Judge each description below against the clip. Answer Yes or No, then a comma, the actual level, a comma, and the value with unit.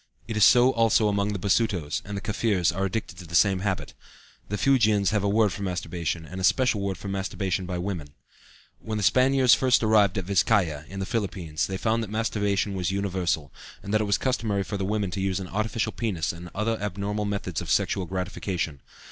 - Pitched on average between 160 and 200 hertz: No, low, 100 Hz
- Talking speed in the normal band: No, fast, 210 wpm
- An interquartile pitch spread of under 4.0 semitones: Yes, average, 2.7 semitones